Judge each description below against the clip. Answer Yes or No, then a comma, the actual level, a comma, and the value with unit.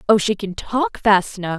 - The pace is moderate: No, fast, 225 wpm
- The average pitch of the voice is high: Yes, high, 200 Hz